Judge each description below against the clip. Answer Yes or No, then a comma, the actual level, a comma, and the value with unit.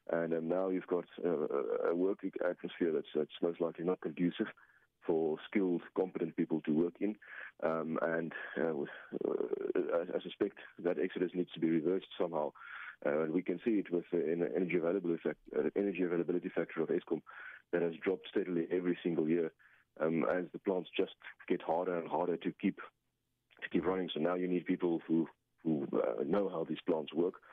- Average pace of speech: Yes, average, 195 wpm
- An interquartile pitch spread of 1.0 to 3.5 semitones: Yes, narrow, 2.4 semitones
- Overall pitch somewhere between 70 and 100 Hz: Yes, very low, 90 Hz